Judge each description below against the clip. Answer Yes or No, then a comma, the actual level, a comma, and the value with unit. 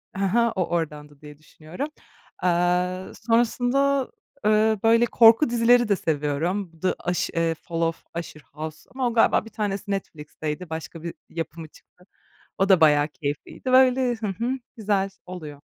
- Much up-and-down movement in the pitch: Yes, wide, 6.0 semitones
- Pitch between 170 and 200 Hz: Yes, medium, 185 Hz